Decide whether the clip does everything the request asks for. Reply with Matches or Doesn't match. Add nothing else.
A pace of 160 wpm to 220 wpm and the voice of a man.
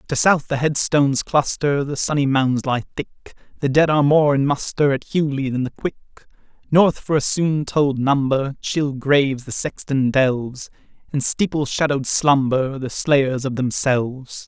Matches